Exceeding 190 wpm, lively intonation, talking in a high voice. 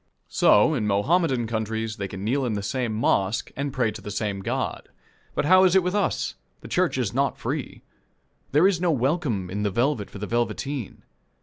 No: average, 200 wpm; wide, 6.1 semitones; low, 120 Hz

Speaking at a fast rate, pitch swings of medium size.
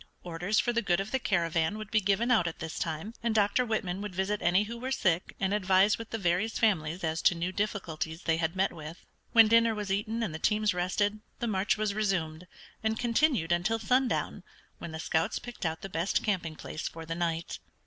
Yes: fast, 220 wpm; average, 4.3 semitones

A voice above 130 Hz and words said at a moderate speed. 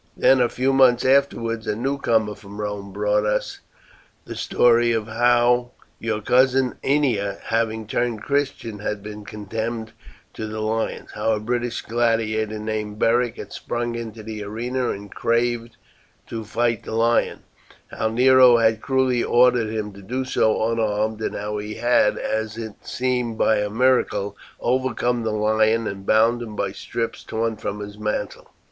No: low, 115 Hz; average, 160 wpm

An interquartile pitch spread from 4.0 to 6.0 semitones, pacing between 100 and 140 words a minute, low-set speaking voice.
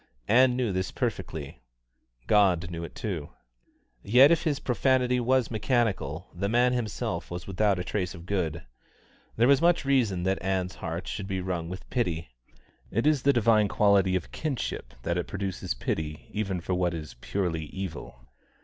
No: wide, 5.6 semitones; average, 165 wpm; very low, 95 Hz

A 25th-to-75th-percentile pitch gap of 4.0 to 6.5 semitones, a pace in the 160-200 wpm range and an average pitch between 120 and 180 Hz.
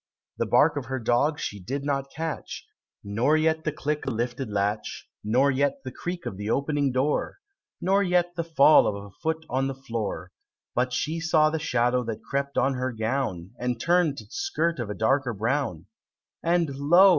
Yes: average, 4.8 semitones; average, 190 wpm; low, 135 Hz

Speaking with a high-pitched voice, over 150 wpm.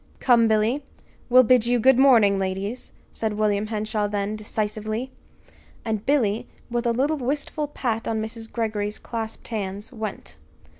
No: high, 220 Hz; average, 145 wpm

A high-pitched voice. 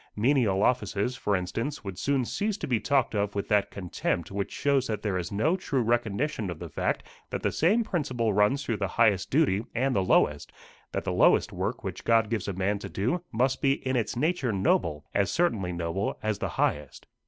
No: low, 110 Hz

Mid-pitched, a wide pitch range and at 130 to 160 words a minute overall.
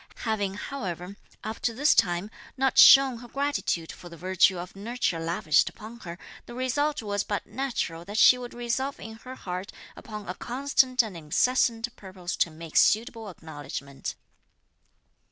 No: high, 215 Hz; wide, 5.9 semitones; average, 155 wpm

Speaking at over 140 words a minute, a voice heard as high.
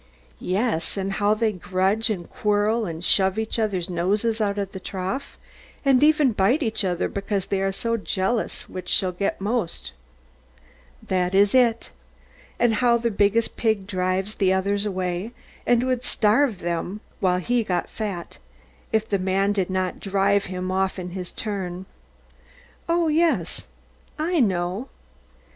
Yes: average, 155 wpm; high, 200 Hz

